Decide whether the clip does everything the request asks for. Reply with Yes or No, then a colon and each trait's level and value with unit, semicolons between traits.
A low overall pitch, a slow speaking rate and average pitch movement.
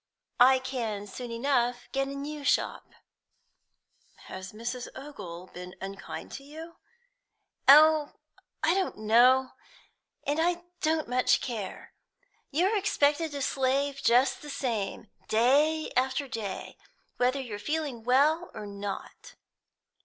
No: very high, 265 Hz; slow, 120 wpm; average, 4.3 semitones